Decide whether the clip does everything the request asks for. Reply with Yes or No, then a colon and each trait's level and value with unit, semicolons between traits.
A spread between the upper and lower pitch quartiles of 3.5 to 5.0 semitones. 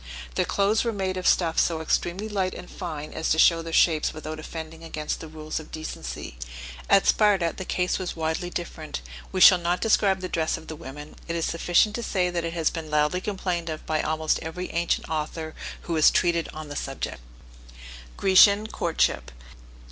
No: average, 2.7 semitones